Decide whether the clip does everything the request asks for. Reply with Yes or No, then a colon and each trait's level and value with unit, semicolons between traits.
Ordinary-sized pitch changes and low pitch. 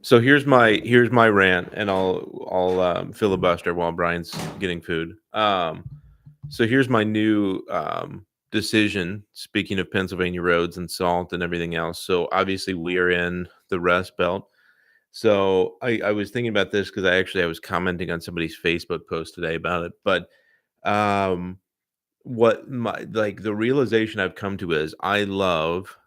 Yes: average, 3.4 semitones; very low, 95 Hz